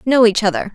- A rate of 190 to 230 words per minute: No, fast, 240 wpm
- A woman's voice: Yes, female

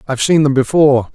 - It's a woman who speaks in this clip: No, male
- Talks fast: Yes, fast, 265 wpm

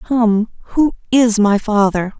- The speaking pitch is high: Yes, high, 220 Hz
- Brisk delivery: No, slow, 135 wpm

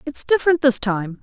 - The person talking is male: No, female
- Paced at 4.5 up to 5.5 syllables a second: Yes, 5.4 syllables/s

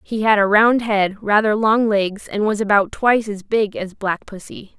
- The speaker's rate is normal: No, fast, 215 wpm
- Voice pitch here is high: Yes, high, 210 Hz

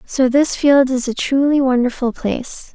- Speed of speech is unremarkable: Yes, average, 175 wpm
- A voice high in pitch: Yes, very high, 265 Hz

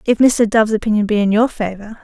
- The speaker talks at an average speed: No, fast, 235 wpm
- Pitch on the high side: Yes, high, 215 Hz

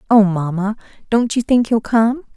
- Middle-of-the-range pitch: No, high, 220 Hz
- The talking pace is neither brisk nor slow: Yes, average, 180 wpm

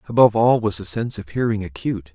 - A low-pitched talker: Yes, low, 100 Hz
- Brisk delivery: Yes, fast, 225 wpm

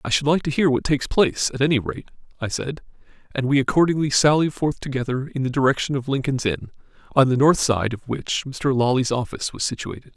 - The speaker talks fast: Yes, fast, 215 wpm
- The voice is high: No, low, 135 Hz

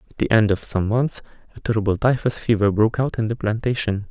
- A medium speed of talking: No, fast, 220 wpm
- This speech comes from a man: Yes, male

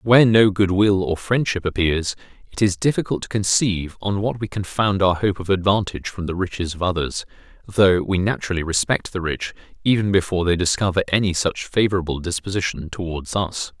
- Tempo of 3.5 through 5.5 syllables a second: No, 5.7 syllables/s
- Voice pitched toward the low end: Yes, very low, 95 Hz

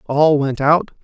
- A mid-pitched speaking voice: Yes, medium, 150 Hz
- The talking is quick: No, average, 175 wpm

